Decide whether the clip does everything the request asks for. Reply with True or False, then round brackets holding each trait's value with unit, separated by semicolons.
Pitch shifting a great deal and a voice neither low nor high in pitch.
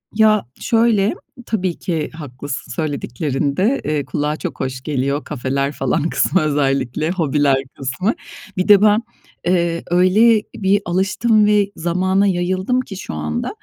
True (6.1 semitones; 170 Hz)